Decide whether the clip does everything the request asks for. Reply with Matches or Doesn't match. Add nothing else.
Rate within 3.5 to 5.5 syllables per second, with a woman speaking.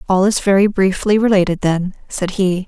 Matches